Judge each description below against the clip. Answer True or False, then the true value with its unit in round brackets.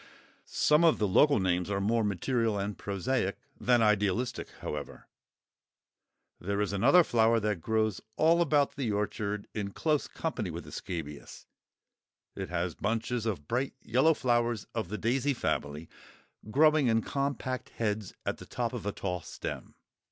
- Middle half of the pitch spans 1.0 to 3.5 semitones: False (4.4 semitones)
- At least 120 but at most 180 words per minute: True (150 wpm)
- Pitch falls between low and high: False (110 Hz)